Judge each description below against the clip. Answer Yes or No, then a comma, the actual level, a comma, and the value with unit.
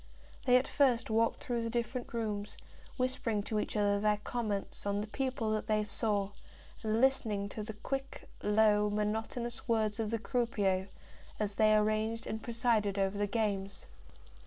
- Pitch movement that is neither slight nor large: No, narrow, 2.1 semitones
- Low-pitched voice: No, high, 215 Hz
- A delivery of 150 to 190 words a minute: Yes, average, 160 wpm